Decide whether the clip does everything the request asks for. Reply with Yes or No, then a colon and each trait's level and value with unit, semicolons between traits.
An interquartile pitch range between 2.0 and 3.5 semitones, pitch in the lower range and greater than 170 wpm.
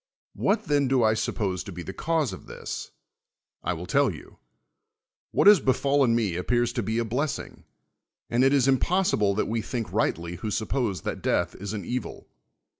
No: average, 4.7 semitones; low, 120 Hz; average, 185 wpm